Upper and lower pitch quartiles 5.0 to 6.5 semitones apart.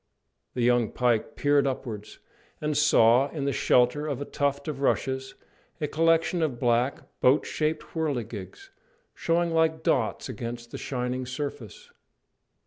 No: average, 3.7 semitones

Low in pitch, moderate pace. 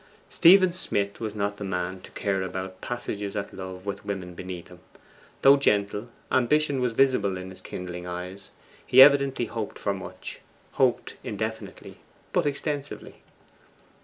Yes: low, 100 Hz; average, 145 wpm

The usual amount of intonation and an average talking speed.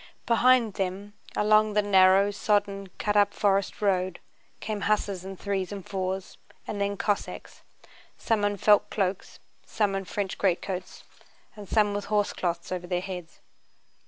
No: narrow, 1.6 semitones; average, 145 wpm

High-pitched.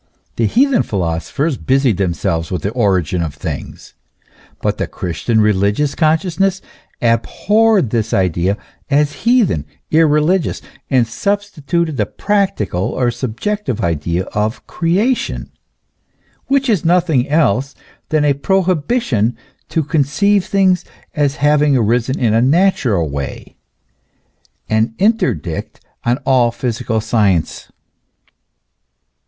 No: low, 135 Hz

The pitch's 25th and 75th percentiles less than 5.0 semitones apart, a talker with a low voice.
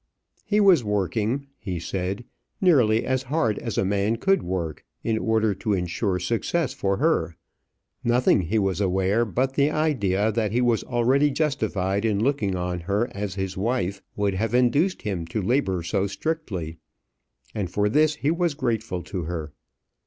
No: average, 5.3 semitones; low, 110 Hz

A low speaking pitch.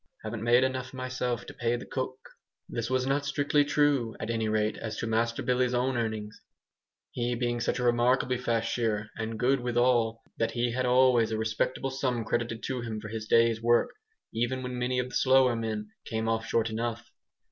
Yes: low, 120 Hz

